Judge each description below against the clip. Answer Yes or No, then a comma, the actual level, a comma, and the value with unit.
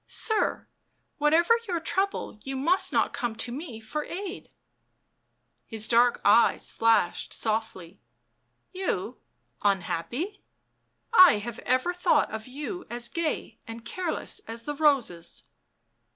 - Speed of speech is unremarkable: No, slow, 125 wpm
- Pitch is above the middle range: Yes, very high, 255 Hz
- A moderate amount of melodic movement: No, wide, 7.2 semitones